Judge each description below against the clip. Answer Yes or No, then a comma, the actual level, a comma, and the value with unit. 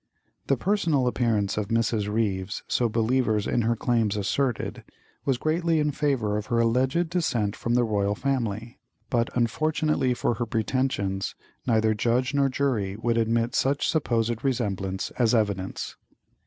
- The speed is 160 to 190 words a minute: No, average, 145 wpm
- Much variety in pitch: No, average, 3.7 semitones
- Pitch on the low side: Yes, low, 115 Hz